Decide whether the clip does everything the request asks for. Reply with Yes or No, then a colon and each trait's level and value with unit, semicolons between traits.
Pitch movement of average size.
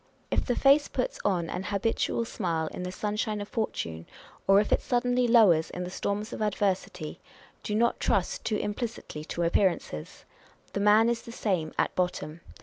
Yes: average, 4.2 semitones